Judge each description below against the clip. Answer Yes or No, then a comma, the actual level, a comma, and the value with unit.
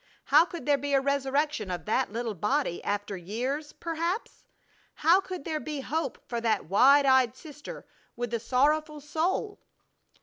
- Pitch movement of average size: Yes, average, 4.7 semitones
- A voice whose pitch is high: Yes, very high, 280 Hz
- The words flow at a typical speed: Yes, average, 160 wpm